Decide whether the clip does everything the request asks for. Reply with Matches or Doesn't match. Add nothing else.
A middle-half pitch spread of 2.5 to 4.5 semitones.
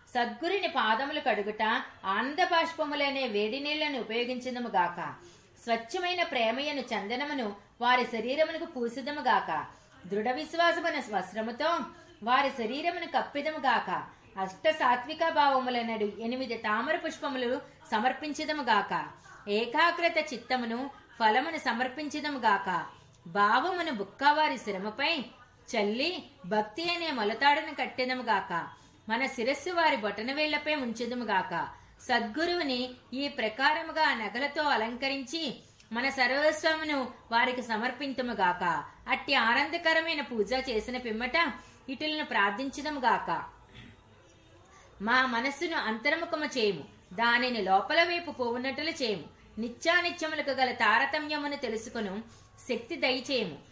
Doesn't match